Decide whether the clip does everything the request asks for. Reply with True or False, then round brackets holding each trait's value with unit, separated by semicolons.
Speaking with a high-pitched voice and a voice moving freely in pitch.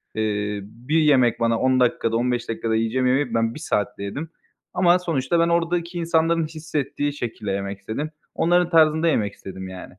False (130 Hz; 6.6 semitones)